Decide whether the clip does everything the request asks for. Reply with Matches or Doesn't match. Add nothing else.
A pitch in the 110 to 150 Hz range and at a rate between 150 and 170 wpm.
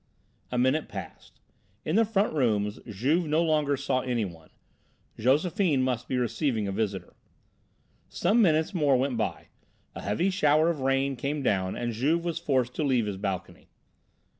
Matches